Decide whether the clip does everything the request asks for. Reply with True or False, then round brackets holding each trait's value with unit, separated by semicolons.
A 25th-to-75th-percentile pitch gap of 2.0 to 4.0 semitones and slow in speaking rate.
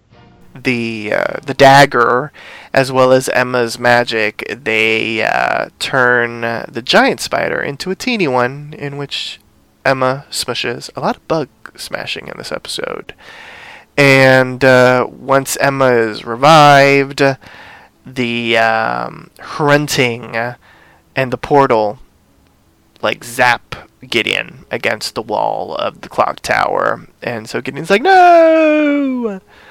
True (3.4 semitones; 120 wpm)